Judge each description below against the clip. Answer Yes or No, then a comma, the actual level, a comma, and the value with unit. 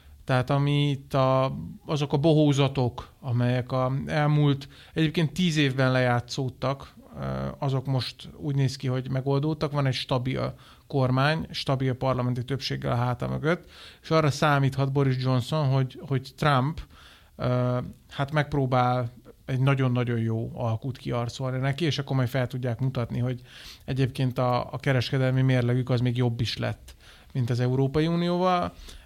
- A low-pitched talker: Yes, low, 130 Hz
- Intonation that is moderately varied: No, narrow, 2.1 semitones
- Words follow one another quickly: No, average, 140 wpm